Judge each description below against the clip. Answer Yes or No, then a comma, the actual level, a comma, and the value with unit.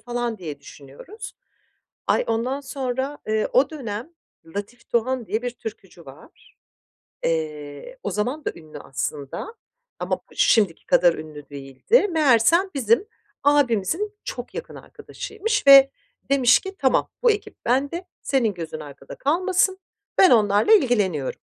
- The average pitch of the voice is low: No, high, 240 Hz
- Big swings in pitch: Yes, wide, 8.6 semitones